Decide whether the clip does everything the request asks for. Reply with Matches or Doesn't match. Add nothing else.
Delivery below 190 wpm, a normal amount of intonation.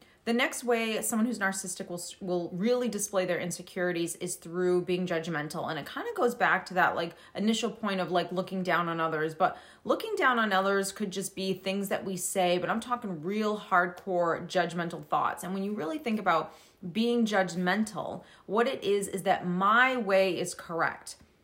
Doesn't match